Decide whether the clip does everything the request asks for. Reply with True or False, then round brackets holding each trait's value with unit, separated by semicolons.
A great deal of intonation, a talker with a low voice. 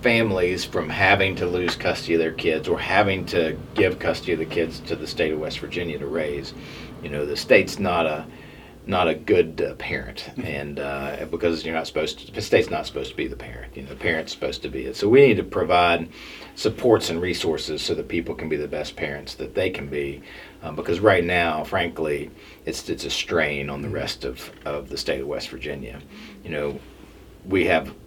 False (3.8 semitones; 80 Hz)